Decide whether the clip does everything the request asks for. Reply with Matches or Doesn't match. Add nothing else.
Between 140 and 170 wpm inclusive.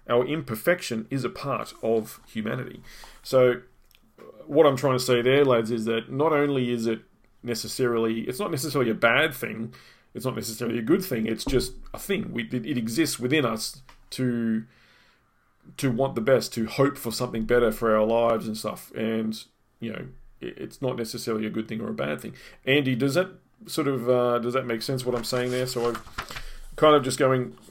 Doesn't match